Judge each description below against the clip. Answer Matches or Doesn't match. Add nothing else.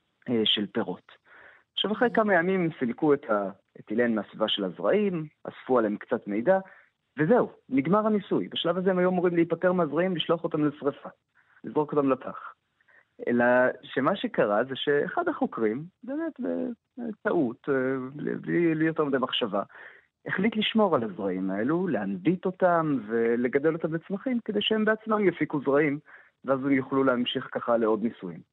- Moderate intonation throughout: Doesn't match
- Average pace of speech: Matches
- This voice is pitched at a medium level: Matches